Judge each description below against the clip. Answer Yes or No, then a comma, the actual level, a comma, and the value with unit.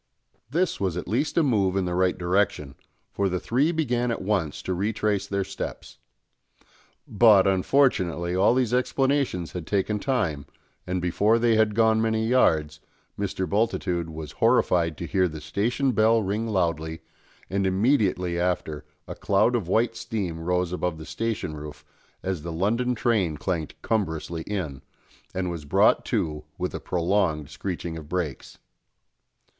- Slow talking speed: No, average, 155 wpm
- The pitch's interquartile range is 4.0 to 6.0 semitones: Yes, average, 4.7 semitones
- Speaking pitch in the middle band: No, very low, 95 Hz